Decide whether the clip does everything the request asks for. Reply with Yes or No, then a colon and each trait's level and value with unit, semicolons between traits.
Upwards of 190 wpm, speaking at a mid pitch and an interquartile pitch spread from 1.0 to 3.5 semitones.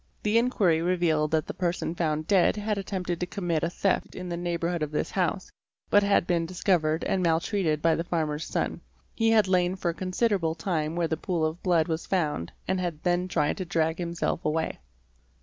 Yes: average, 200 wpm; medium, 175 Hz; narrow, 2.5 semitones